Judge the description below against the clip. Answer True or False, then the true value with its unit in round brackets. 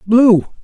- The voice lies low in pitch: False (225 Hz)